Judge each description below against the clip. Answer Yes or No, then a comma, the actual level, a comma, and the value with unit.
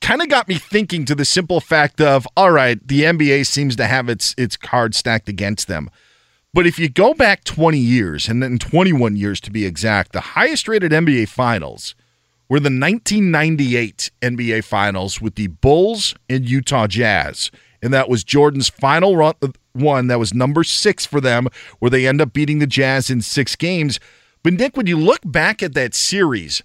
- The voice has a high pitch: No, low, 135 Hz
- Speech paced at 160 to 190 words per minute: No, average, 200 wpm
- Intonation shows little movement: No, average, 5.0 semitones